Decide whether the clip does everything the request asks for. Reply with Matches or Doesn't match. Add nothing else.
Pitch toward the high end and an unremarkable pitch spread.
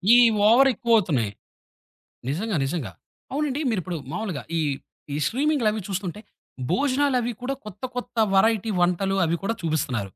Doesn't match